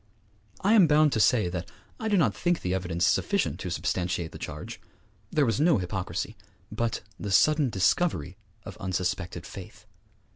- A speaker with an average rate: Yes, average, 160 wpm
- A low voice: Yes, low, 105 Hz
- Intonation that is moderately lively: No, wide, 9.0 semitones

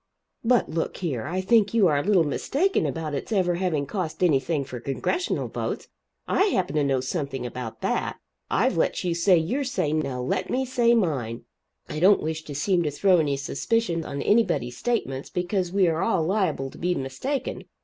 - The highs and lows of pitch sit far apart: Yes, wide, 6.1 semitones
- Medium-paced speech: Yes, average, 190 wpm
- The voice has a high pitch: No, medium, 170 Hz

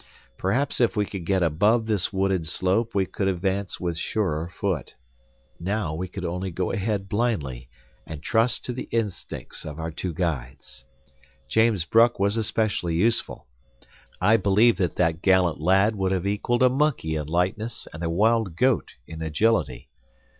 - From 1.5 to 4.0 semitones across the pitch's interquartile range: No, average, 4.8 semitones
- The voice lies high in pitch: No, very low, 95 Hz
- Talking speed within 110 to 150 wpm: No, average, 160 wpm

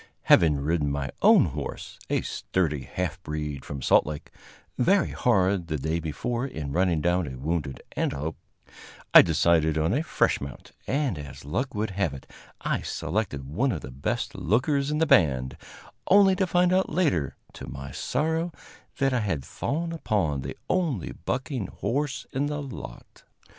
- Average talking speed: Yes, average, 165 wpm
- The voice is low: Yes, very low, 90 Hz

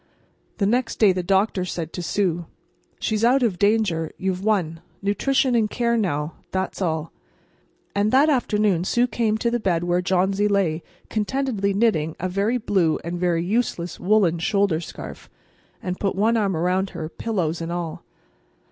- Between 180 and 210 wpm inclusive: No, average, 160 wpm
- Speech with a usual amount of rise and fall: Yes, average, 3.9 semitones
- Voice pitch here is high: Yes, high, 195 Hz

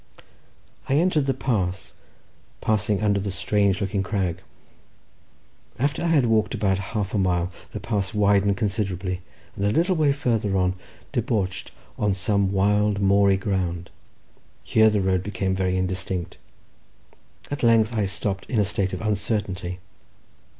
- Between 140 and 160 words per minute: Yes, average, 145 wpm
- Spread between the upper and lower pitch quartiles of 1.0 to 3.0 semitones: Yes, narrow, 2.4 semitones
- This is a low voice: Yes, low, 100 Hz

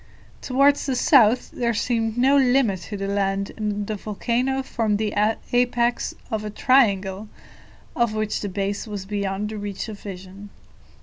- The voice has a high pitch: Yes, high, 215 Hz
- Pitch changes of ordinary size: Yes, average, 3.4 semitones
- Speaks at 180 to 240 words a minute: No, average, 160 wpm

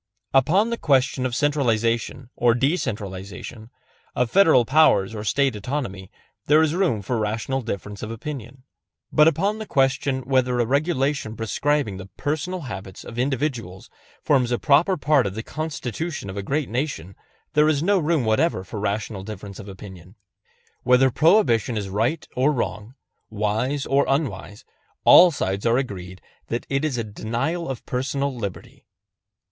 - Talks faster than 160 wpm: No, average, 155 wpm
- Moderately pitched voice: No, low, 125 Hz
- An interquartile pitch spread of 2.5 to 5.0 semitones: No, wide, 5.6 semitones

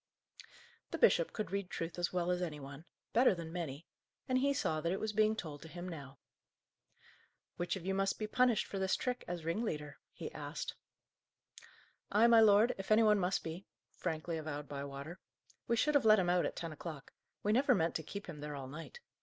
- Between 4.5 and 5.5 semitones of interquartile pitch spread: Yes, average, 5.2 semitones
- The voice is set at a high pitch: No, medium, 180 Hz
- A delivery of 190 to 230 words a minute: Yes, fast, 205 wpm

